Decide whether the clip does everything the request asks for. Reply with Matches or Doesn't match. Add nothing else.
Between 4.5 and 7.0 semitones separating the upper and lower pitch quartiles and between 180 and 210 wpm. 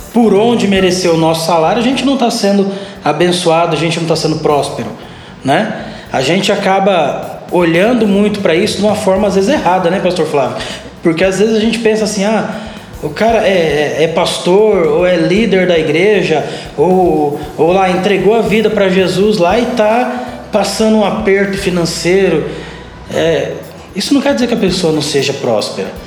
Doesn't match